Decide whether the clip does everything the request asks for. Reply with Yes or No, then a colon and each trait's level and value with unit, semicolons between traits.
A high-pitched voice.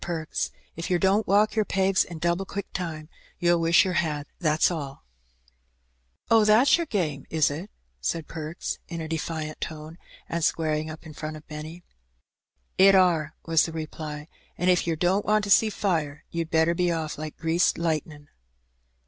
No: medium, 165 Hz